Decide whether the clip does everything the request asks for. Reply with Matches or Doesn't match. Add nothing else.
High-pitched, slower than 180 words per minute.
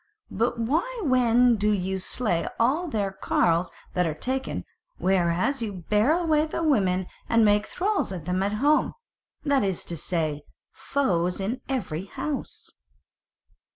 Matches